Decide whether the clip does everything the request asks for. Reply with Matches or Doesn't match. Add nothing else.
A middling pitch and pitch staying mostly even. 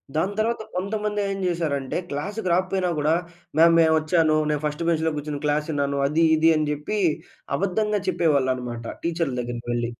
Doesn't match